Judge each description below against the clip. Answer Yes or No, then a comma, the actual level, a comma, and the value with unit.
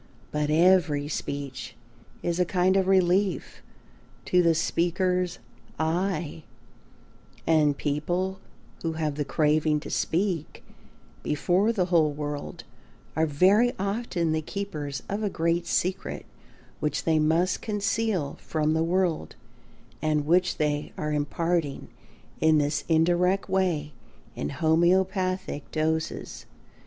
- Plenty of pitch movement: No, average, 3.5 semitones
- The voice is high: No, medium, 165 Hz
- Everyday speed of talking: No, slow, 115 wpm